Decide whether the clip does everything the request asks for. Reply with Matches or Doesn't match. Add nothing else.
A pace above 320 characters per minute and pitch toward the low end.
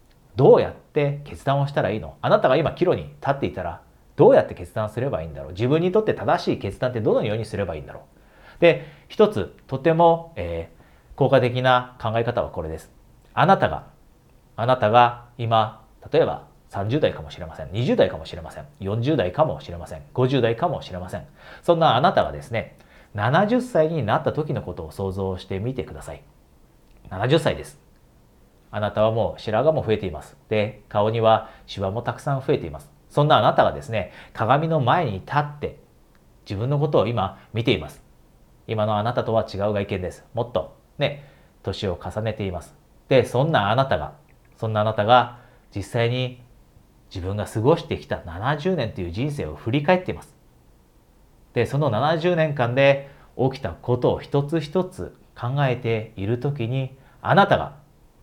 Matches